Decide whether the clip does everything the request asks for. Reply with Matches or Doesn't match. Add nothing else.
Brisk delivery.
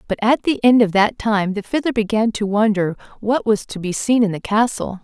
Matches